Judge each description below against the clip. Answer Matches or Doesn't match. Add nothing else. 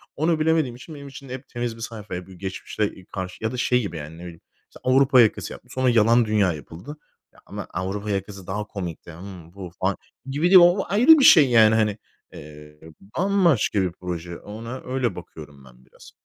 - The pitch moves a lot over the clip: Matches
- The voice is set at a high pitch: Doesn't match